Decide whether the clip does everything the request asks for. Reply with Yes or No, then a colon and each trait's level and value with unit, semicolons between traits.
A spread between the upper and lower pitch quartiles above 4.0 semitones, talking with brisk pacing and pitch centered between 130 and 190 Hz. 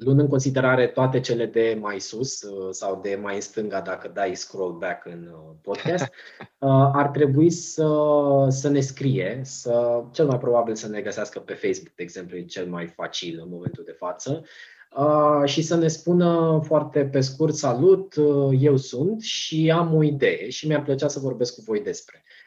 Yes: average, 4.7 semitones; fast, 175 wpm; medium, 140 Hz